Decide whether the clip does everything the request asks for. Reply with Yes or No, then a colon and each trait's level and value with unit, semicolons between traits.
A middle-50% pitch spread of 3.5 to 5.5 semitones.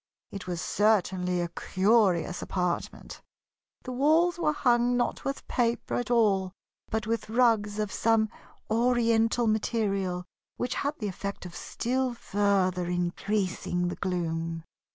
Yes: average, 4.7 semitones